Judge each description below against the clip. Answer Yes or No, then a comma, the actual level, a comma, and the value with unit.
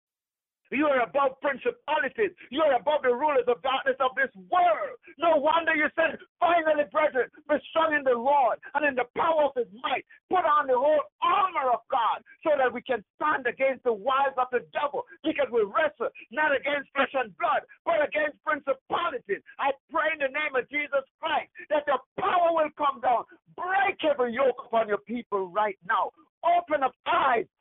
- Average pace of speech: Yes, average, 185 wpm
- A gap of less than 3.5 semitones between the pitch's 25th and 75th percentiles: No, average, 3.8 semitones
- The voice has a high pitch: Yes, very high, 295 Hz